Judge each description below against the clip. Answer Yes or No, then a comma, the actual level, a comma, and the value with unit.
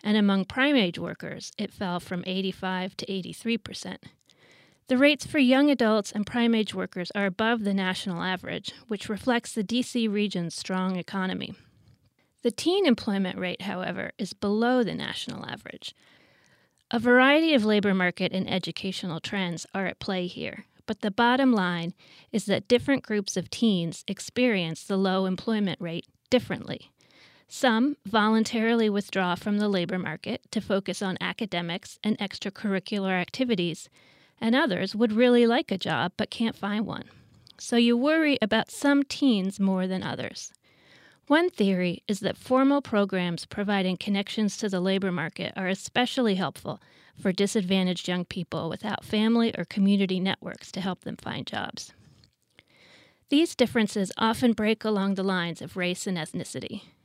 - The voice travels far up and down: No, average, 3.8 semitones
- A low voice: No, high, 200 Hz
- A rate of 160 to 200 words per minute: No, average, 150 wpm